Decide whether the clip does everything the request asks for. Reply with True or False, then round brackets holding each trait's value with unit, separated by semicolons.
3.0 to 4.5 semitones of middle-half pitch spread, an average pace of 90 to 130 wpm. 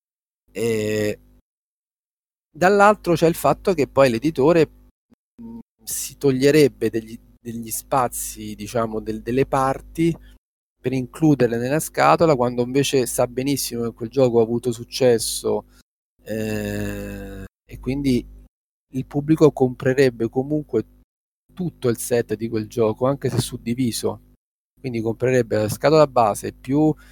True (3.6 semitones; 115 wpm)